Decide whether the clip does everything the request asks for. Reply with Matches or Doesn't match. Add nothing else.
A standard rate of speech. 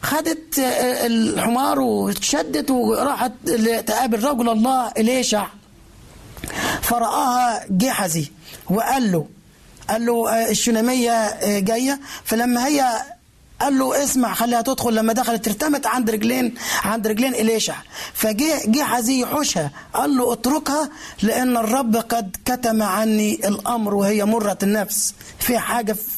Matches